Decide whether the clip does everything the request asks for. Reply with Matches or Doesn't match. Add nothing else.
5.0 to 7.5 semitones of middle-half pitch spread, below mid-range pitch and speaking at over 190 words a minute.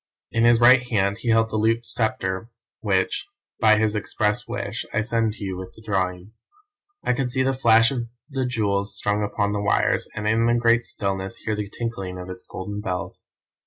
Doesn't match